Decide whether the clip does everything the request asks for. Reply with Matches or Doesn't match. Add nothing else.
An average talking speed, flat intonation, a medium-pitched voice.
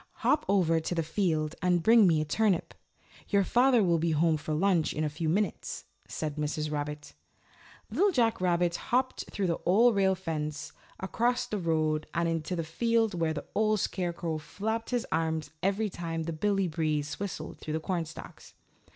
Doesn't match